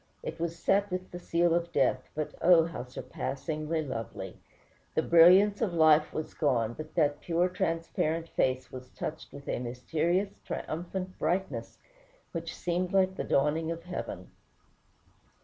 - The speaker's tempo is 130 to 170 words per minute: Yes, average, 150 wpm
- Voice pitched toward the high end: No, medium, 165 Hz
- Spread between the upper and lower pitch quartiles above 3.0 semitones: No, average, 2.7 semitones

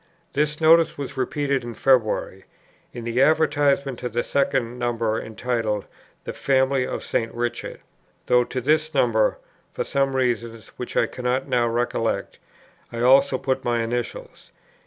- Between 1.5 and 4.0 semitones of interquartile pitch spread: Yes, narrow, 2.6 semitones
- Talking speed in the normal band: Yes, average, 145 wpm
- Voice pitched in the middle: No, low, 125 Hz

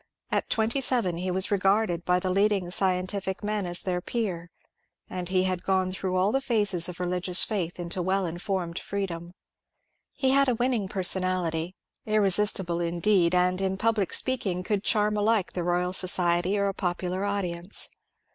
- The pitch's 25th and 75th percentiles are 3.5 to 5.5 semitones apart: No, narrow, 2.5 semitones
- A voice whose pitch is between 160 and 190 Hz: Yes, medium, 185 Hz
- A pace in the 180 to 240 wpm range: No, average, 165 wpm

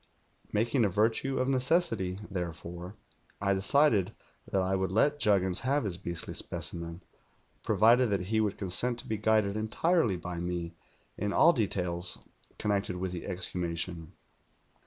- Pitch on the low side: Yes, low, 100 Hz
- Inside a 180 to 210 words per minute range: No, average, 145 wpm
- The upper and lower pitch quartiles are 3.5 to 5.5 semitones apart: Yes, average, 4.0 semitones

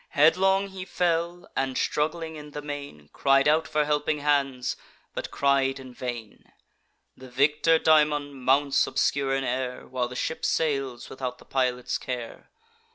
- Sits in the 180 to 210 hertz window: No, medium, 140 Hz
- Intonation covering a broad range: No, average, 2.8 semitones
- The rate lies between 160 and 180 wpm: No, average, 150 wpm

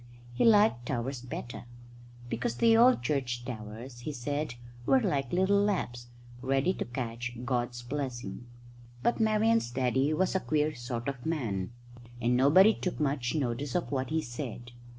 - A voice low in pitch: Yes, low, 130 Hz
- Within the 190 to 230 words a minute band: No, average, 150 wpm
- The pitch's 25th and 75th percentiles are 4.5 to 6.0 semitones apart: Yes, average, 4.9 semitones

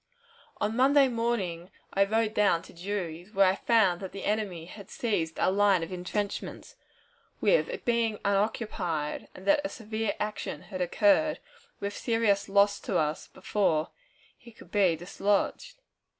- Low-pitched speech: No, high, 205 Hz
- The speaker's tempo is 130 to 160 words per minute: Yes, average, 150 wpm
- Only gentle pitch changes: No, average, 3.7 semitones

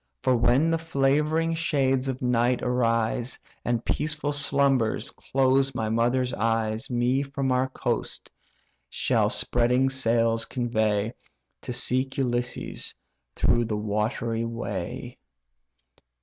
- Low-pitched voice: Yes, low, 125 Hz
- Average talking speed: No, slow, 110 wpm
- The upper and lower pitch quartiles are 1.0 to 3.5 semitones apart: Yes, average, 2.7 semitones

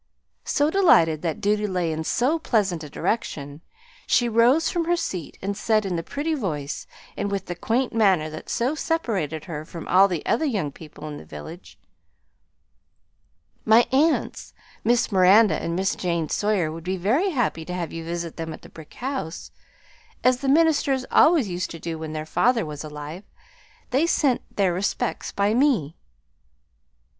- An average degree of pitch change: No, wide, 7.5 semitones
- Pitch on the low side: No, high, 195 Hz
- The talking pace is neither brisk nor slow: Yes, average, 170 wpm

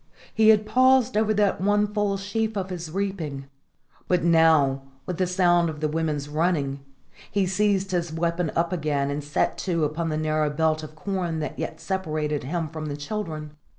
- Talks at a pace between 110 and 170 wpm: No, average, 180 wpm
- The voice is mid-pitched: Yes, medium, 170 Hz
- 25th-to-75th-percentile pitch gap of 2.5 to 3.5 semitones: No, average, 4.1 semitones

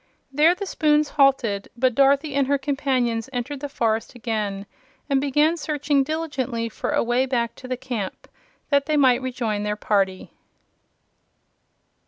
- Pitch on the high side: Yes, very high, 260 Hz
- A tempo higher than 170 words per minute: No, average, 150 wpm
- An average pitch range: Yes, average, 3.7 semitones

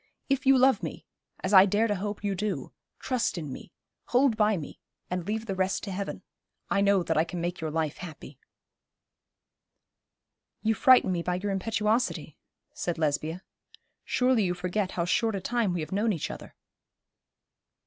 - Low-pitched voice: No, high, 195 Hz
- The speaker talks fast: No, average, 175 wpm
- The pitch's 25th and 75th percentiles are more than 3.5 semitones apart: Yes, average, 4.0 semitones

